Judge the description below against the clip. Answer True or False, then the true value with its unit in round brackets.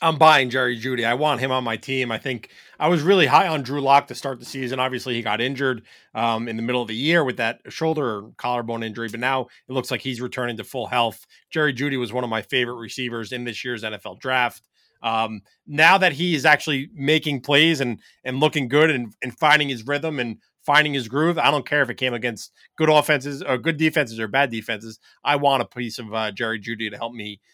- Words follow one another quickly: True (240 wpm)